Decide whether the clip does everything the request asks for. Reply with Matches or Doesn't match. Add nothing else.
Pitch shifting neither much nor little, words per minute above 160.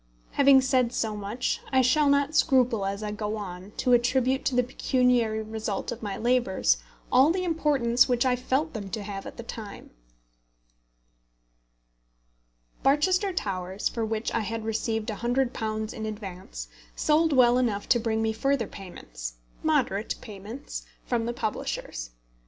Doesn't match